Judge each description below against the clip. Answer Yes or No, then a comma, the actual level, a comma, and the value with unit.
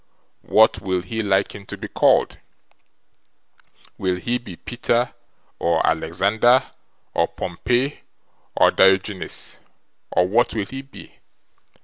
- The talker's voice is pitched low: Yes, low, 100 Hz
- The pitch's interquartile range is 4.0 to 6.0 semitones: Yes, average, 4.6 semitones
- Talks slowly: Yes, slow, 115 wpm